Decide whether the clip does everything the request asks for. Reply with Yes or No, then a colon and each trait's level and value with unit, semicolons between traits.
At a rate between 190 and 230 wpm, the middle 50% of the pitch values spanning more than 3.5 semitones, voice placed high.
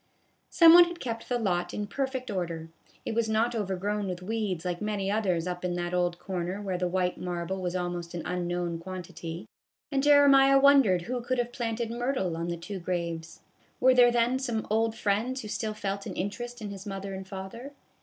Yes: fast, 205 wpm; average, 5.1 semitones; high, 200 Hz